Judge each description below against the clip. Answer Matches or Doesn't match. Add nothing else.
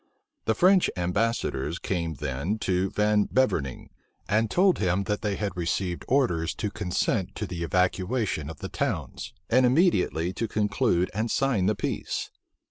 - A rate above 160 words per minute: Doesn't match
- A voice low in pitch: Matches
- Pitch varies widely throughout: Doesn't match